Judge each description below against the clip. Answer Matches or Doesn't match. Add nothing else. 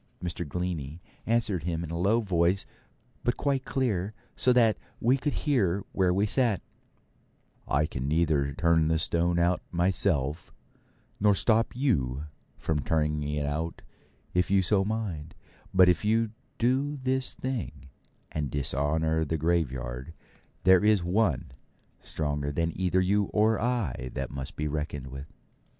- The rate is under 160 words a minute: Matches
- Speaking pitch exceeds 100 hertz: Doesn't match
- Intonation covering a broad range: Matches